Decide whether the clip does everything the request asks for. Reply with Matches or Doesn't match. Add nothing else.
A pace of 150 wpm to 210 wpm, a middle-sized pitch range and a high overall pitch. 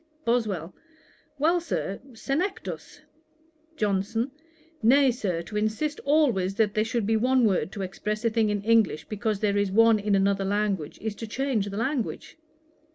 Matches